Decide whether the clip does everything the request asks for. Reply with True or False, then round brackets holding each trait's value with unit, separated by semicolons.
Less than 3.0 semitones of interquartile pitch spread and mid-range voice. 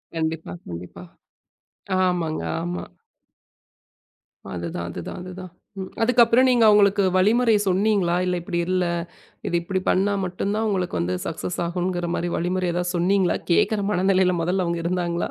True (2.5 semitones; 180 Hz)